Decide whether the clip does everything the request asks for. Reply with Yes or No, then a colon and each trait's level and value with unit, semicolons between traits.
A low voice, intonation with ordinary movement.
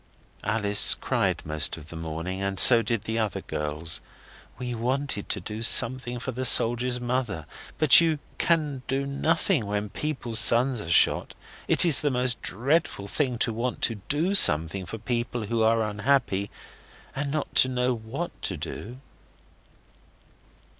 Yes: low, 120 Hz; average, 4.4 semitones